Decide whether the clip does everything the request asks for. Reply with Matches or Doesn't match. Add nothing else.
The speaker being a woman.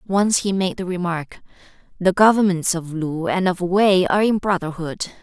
Matches